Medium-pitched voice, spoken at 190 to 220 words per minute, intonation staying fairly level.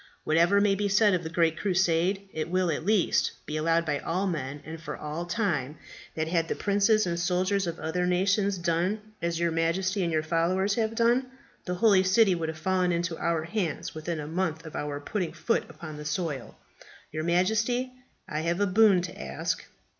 No: medium, 175 Hz; average, 200 wpm; average, 3.4 semitones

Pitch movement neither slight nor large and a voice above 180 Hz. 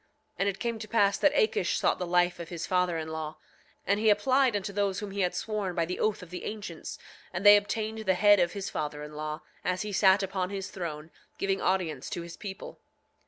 Yes: average, 3.0 semitones; high, 190 Hz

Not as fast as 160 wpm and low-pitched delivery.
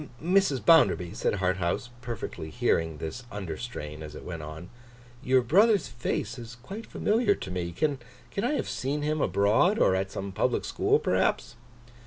No: average, 165 wpm; low, 120 Hz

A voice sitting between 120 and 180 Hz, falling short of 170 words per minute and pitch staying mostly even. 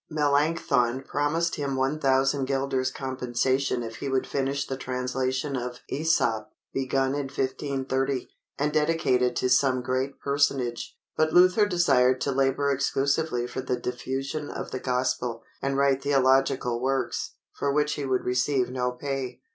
Yes: low, 135 Hz; average, 145 wpm; narrow, 1.8 semitones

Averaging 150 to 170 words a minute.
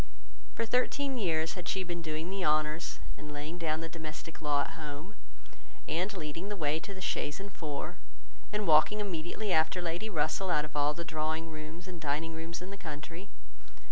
No: average, 190 wpm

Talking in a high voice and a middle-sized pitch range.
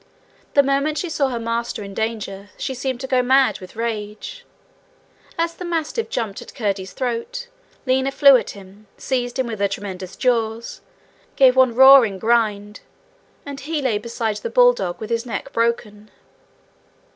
Yes: high, 235 Hz; average, 4.3 semitones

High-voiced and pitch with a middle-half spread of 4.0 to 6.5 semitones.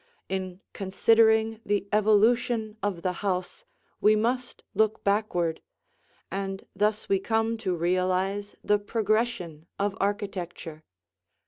No: high, 205 Hz; average, 2.9 semitones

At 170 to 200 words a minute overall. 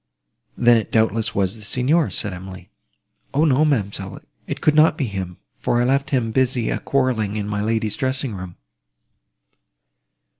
No: average, 160 wpm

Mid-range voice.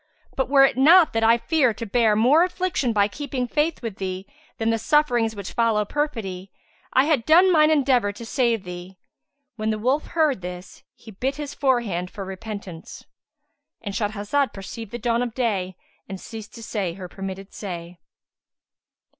No: high, 225 Hz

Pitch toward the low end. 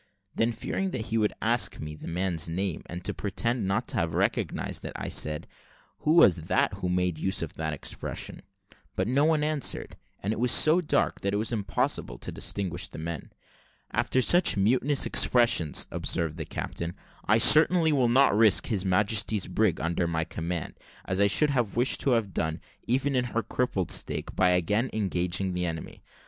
Yes: low, 100 Hz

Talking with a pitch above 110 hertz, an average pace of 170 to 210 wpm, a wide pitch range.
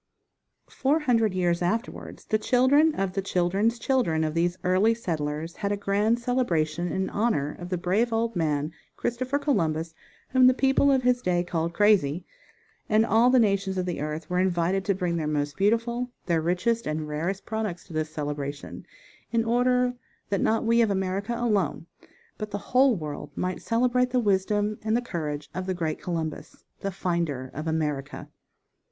Yes: high, 190 Hz; average, 175 wpm; wide, 5.9 semitones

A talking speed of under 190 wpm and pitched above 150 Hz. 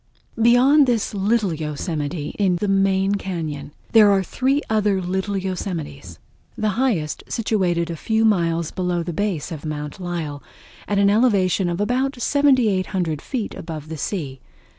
Yes: average, 145 wpm; high, 190 Hz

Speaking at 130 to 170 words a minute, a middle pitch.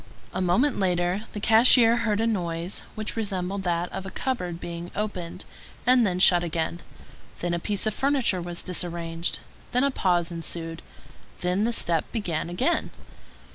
Yes: average, 160 wpm; medium, 180 Hz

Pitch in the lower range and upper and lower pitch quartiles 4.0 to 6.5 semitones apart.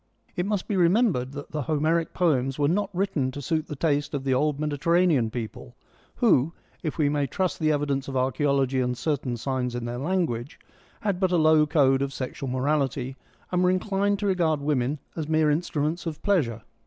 No: medium, 150 Hz; average, 4.3 semitones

